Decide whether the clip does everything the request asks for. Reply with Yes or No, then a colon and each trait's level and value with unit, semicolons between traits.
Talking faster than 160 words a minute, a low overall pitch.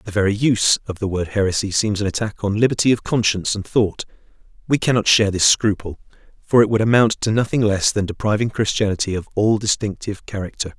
Yes: average, 195 wpm; low, 105 Hz